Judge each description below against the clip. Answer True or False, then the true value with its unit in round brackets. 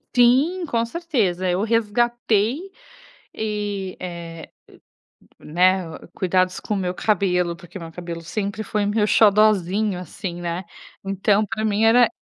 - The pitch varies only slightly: False (3.5 semitones)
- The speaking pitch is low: False (200 Hz)